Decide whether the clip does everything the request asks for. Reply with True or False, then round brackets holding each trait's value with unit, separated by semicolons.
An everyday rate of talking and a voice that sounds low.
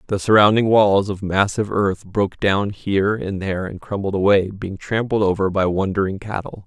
True (180 wpm; 100 Hz)